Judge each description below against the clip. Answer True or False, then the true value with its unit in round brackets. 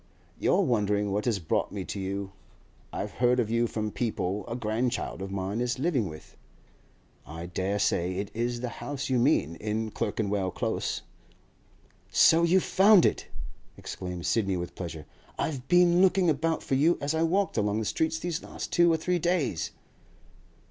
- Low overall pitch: True (115 Hz)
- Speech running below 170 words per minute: False (175 wpm)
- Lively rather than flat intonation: True (8.3 semitones)